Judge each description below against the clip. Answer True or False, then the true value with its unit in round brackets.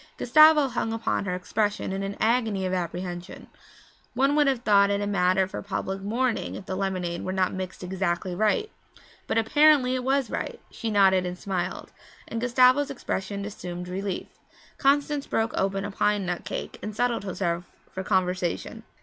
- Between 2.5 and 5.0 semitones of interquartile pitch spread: True (4.4 semitones)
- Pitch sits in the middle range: False (200 Hz)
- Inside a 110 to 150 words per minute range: False (170 wpm)